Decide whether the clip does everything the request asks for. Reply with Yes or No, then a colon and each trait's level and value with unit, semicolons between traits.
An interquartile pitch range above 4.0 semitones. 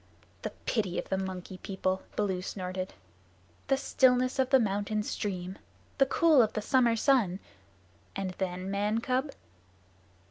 Yes: average, 5.2 semitones